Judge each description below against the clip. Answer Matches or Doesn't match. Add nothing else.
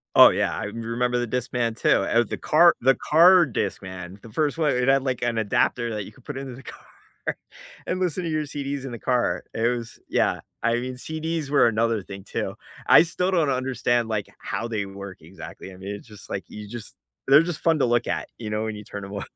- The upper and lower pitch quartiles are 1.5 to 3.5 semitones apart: Doesn't match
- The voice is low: Matches